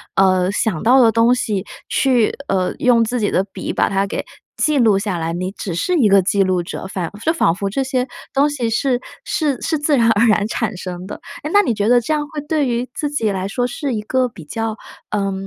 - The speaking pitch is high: Yes, high, 225 Hz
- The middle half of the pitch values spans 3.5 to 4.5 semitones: No, average, 5.0 semitones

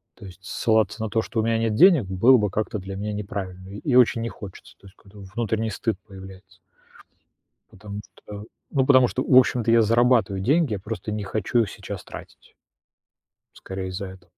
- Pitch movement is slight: No, average, 3.1 semitones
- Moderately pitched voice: No, low, 105 Hz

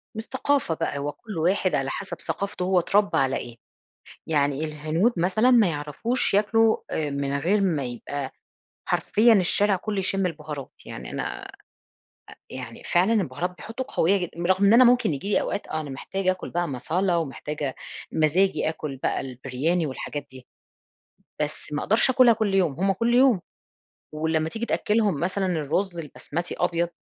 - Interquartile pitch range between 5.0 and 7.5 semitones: Yes, wide, 5.4 semitones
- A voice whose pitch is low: No, medium, 175 Hz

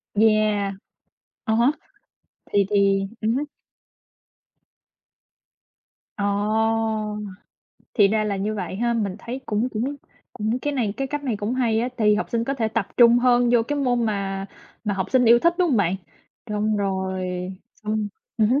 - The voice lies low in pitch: No, high, 220 Hz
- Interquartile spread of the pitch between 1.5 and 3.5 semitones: Yes, average, 3.1 semitones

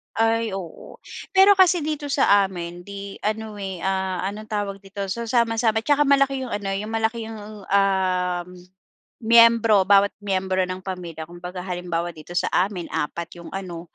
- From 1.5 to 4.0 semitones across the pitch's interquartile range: Yes, average, 3.7 semitones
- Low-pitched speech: No, high, 200 Hz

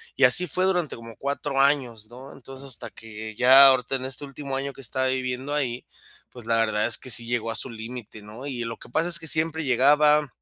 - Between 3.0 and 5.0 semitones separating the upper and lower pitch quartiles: Yes, average, 3.4 semitones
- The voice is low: Yes, low, 130 Hz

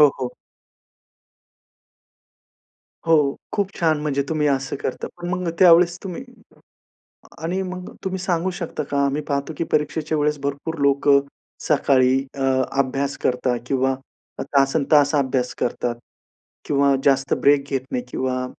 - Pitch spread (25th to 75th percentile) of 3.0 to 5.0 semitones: Yes, average, 3.4 semitones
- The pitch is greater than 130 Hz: Yes, medium, 140 Hz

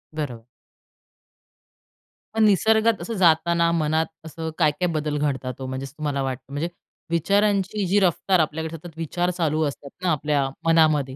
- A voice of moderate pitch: Yes, medium, 160 Hz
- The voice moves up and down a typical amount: Yes, average, 3.4 semitones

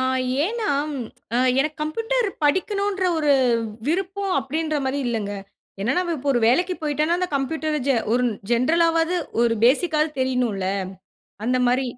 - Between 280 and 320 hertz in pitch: Yes, very high, 305 Hz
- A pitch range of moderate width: No, wide, 5.8 semitones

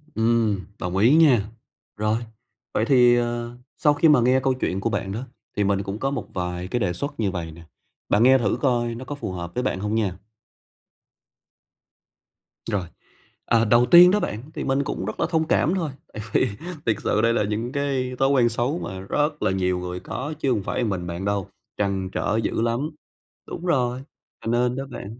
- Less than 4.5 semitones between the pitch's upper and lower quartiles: No, average, 5.0 semitones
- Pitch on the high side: No, low, 115 Hz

